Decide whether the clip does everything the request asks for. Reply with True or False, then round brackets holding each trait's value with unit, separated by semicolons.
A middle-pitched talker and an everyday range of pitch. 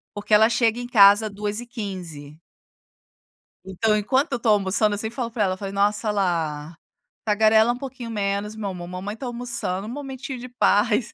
False (210 Hz; 3.1 semitones)